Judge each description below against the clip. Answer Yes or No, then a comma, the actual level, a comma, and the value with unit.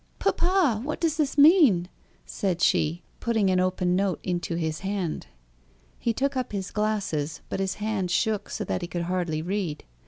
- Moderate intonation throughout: Yes, average, 4.3 semitones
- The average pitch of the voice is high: Yes, high, 195 Hz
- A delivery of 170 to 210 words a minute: Yes, average, 175 wpm